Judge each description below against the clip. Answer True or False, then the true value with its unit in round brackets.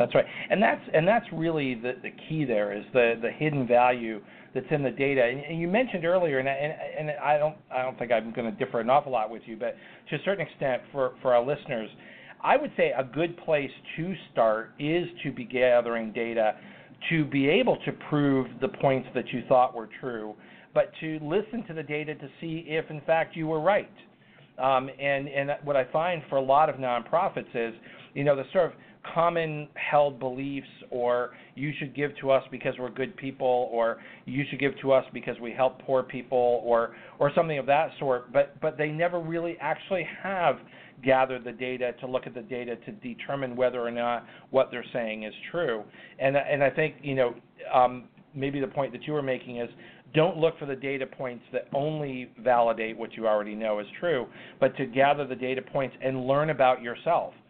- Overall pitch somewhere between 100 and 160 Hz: True (135 Hz)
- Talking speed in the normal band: False (210 wpm)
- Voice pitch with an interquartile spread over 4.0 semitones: False (3.5 semitones)